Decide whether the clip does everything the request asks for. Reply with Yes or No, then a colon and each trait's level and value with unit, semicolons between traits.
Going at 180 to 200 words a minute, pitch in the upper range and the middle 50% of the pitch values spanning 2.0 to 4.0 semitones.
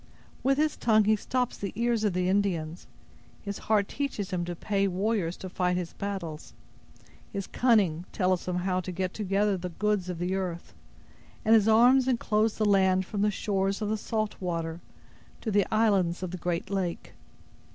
Yes: average, 185 wpm; high, 195 Hz; average, 3.0 semitones